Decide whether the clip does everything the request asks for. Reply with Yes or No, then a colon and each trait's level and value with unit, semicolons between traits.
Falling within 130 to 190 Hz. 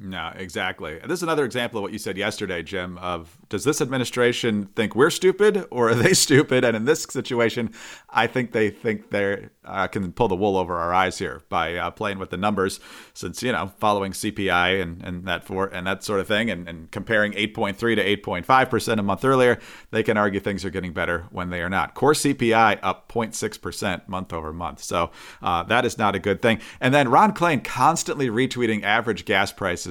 No: low, 105 Hz